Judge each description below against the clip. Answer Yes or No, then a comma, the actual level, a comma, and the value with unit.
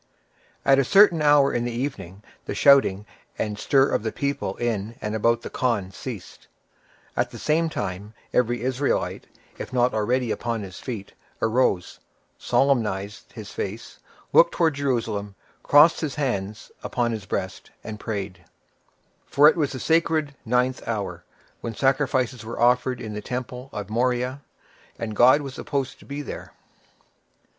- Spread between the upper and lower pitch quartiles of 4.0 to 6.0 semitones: Yes, average, 4.4 semitones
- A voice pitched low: Yes, low, 120 Hz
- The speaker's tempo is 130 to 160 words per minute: Yes, average, 150 wpm